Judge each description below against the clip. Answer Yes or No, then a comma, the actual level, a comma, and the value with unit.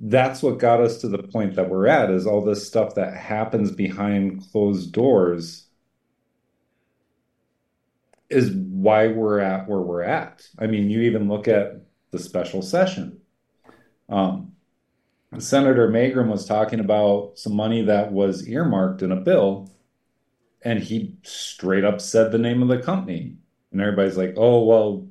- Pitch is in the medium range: No, low, 105 Hz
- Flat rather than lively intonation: No, average, 3.4 semitones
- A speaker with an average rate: Yes, average, 155 wpm